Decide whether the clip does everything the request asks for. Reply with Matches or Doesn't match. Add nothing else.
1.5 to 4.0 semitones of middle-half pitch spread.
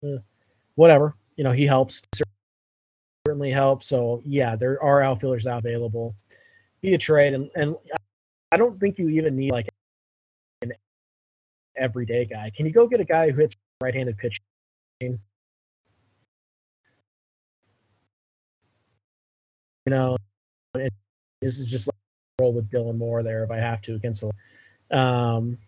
Doesn't match